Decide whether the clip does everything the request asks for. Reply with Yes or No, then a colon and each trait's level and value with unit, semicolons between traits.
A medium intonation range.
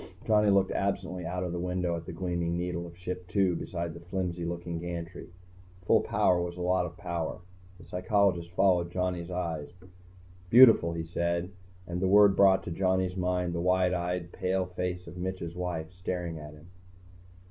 No: narrow, 1.3 semitones